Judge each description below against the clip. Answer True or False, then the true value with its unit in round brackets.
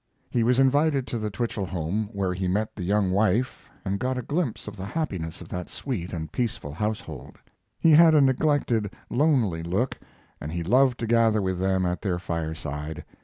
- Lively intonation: True (5.9 semitones)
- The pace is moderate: True (190 wpm)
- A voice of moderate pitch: False (105 Hz)